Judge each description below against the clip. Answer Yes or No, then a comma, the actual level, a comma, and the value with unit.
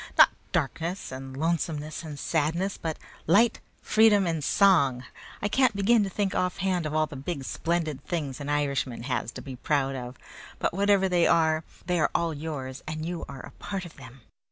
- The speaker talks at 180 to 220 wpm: Yes, average, 185 wpm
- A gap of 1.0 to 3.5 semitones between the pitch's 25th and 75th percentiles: No, average, 4.7 semitones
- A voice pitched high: No, medium, 160 Hz